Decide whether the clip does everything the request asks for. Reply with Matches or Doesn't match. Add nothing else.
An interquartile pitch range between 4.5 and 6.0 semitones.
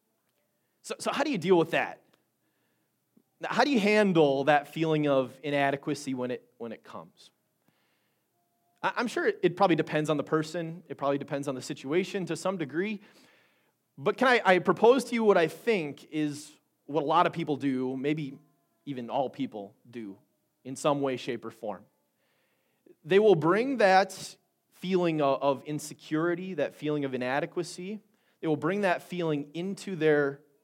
Matches